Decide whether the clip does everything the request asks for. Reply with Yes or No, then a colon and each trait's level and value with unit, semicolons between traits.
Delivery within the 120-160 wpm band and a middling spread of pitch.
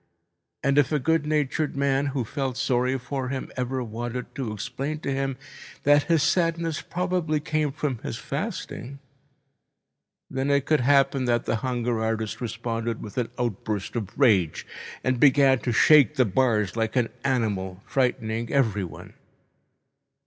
Yes: average, 150 wpm; average, 3.6 semitones